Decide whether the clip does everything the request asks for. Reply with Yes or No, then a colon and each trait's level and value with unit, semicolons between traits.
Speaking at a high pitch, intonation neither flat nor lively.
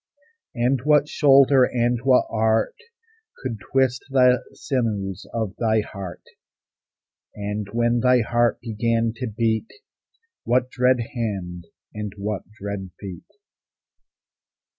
No: low, 115 Hz; average, 3.3 semitones